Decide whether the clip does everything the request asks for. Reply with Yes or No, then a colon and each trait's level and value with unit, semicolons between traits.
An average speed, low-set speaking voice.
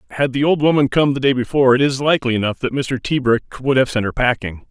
No: fast, 255 wpm; low, 130 Hz